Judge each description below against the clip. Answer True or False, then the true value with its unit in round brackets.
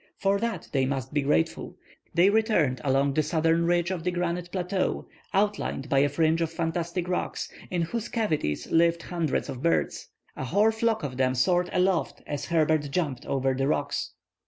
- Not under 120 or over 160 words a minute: False (180 wpm)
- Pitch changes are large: False (4.4 semitones)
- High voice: False (165 Hz)